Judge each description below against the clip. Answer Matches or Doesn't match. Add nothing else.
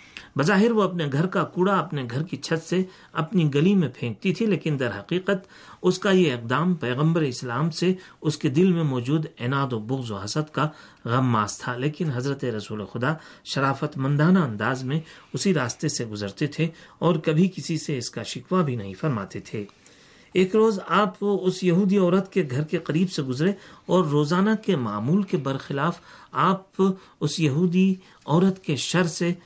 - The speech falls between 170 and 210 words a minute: Matches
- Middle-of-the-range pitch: Matches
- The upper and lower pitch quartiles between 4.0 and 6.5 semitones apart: Matches